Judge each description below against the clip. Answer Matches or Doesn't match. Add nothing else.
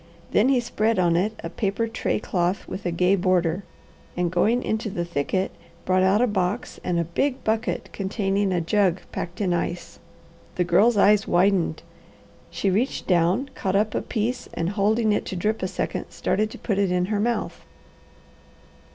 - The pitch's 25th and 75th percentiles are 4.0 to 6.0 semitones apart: Doesn't match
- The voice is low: Doesn't match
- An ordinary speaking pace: Matches